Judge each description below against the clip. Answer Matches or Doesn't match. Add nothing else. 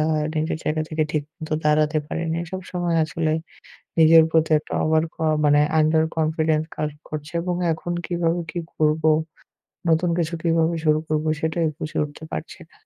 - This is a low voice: Doesn't match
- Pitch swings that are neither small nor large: Doesn't match